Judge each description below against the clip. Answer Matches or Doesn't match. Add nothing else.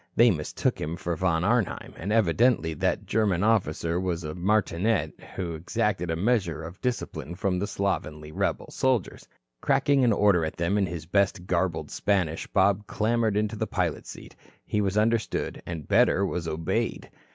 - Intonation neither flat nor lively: Matches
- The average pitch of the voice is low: Matches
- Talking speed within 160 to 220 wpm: Matches